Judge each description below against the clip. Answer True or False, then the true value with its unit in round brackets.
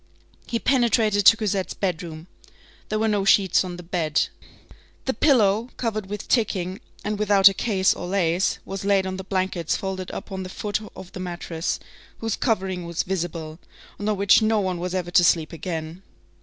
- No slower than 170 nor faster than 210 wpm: True (185 wpm)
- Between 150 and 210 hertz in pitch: True (190 Hz)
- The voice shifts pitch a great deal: False (2.9 semitones)